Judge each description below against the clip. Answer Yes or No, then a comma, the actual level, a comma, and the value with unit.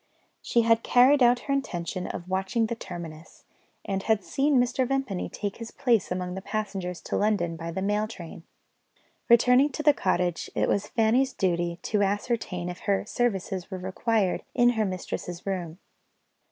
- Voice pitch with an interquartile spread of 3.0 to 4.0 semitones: No, average, 4.7 semitones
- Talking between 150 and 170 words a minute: Yes, average, 165 wpm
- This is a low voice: No, high, 200 Hz